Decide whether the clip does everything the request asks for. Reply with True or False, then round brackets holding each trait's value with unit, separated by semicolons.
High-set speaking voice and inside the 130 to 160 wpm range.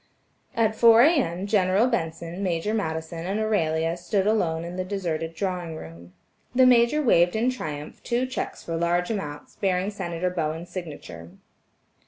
False (180 Hz; 150 wpm)